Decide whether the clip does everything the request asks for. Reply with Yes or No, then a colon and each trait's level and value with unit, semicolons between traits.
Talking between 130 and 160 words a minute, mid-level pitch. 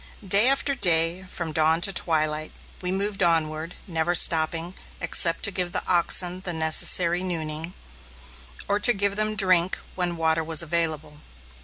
Yes: average, 150 wpm; medium, 170 Hz